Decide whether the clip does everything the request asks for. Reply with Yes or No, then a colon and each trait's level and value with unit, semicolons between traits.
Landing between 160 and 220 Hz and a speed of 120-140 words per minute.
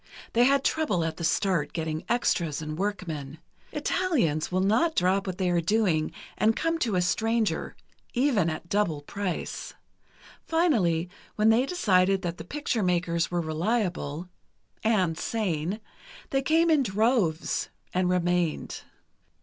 Yes: medium, 185 Hz; slow, 135 wpm